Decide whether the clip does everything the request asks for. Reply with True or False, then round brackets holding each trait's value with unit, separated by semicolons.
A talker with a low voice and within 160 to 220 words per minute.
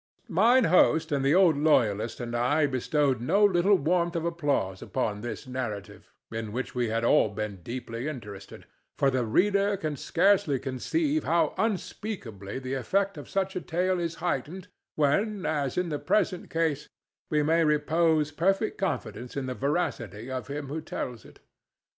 False (150 Hz; 165 wpm)